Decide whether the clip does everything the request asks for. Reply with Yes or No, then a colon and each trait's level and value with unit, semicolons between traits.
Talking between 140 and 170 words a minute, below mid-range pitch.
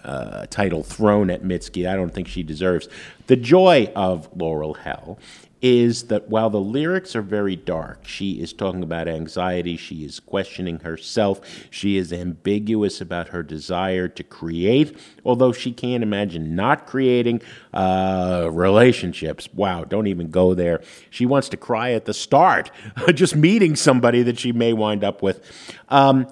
Yes: average, 160 wpm; low, 100 Hz